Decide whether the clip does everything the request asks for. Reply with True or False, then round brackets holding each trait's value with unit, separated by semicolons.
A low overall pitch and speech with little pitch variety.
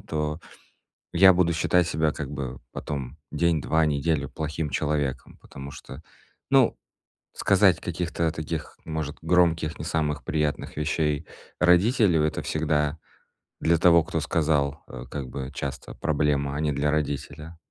True (75 Hz; 2.3 semitones)